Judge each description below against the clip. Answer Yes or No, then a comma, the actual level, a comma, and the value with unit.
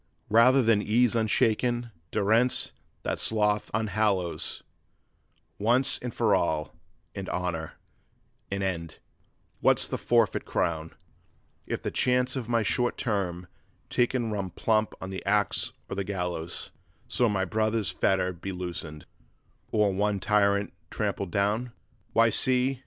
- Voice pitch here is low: Yes, low, 105 Hz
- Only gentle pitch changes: No, average, 3.5 semitones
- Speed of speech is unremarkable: No, slow, 130 wpm